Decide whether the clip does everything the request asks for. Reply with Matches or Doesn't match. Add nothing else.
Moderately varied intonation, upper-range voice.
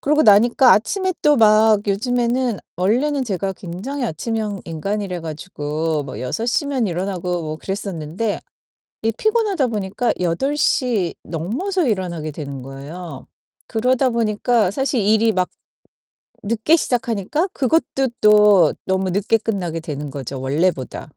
Doesn't match